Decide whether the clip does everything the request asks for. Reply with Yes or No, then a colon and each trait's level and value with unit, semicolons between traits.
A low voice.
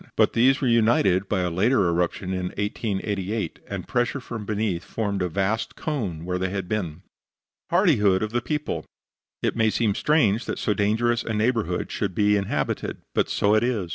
Yes: low, 105 Hz